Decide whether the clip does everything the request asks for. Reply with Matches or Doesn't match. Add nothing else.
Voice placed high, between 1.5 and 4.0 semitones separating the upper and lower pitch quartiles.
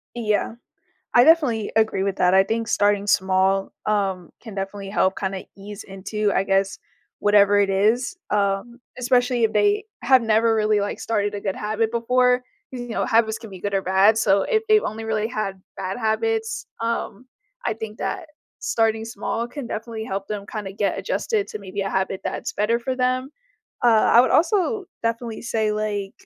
Matches